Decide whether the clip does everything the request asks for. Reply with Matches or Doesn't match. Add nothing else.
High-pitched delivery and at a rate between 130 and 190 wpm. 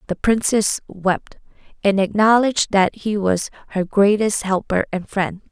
Matches